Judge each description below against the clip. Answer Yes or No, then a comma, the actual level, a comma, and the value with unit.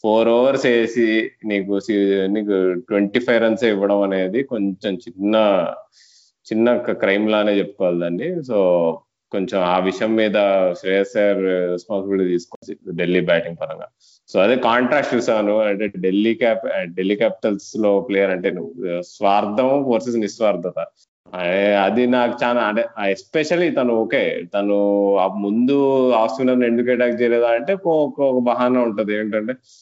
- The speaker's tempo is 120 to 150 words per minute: Yes, fast, 125 wpm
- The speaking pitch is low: Yes, low, 105 Hz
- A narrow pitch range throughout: No, average, 3.4 semitones